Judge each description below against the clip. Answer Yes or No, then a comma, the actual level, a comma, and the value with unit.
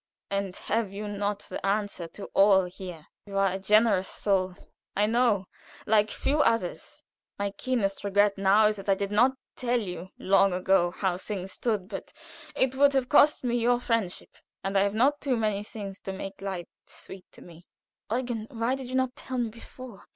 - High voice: Yes, high, 205 Hz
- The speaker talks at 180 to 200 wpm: Yes, average, 190 wpm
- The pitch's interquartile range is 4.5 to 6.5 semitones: No, average, 3.4 semitones